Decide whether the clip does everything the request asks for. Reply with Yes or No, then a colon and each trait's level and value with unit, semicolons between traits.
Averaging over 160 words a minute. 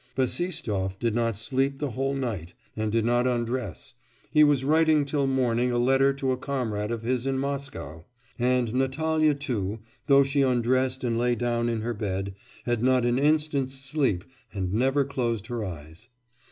Yes: average, 170 wpm